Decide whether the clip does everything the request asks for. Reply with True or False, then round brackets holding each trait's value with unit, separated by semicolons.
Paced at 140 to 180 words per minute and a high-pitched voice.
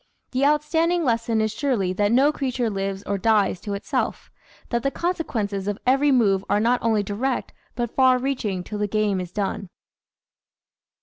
True (175 wpm; 225 Hz)